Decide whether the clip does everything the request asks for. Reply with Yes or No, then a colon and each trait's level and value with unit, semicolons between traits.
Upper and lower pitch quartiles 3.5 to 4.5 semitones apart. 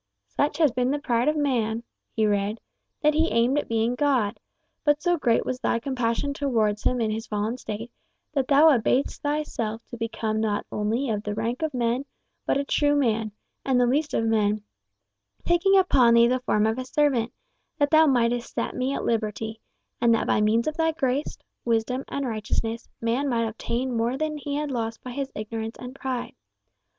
Yes: average, 4.0 semitones